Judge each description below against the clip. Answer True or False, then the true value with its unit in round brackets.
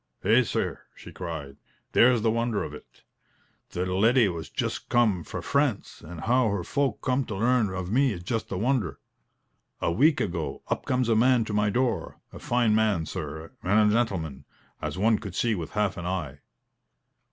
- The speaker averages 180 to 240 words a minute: True (185 wpm)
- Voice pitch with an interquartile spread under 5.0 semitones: False (5.3 semitones)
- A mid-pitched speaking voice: False (105 Hz)